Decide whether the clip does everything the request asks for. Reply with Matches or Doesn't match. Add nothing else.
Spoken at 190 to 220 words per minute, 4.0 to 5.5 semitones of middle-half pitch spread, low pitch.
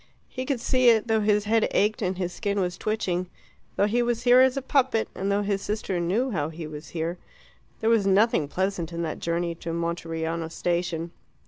Doesn't match